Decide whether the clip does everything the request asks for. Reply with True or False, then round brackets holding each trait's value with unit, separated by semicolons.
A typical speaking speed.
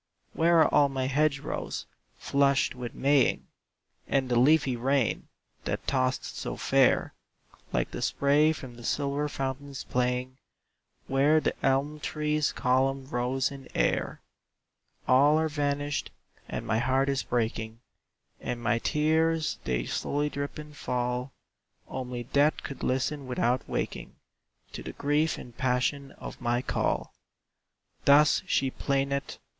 False (130 wpm)